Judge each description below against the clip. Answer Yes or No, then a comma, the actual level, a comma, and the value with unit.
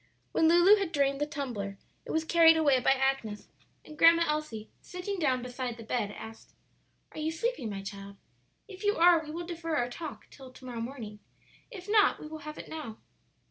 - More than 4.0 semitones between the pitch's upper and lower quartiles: Yes, wide, 5.5 semitones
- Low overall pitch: No, very high, 300 Hz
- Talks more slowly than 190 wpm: No, average, 200 wpm